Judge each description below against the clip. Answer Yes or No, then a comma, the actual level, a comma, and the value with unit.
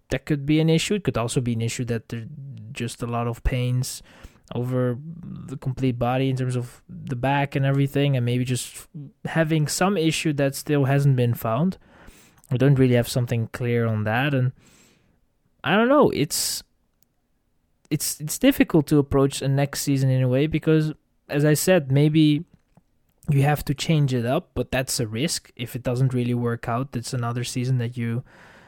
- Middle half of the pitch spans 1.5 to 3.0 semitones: No, average, 3.6 semitones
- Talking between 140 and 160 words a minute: No, average, 190 wpm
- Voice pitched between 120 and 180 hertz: Yes, low, 135 Hz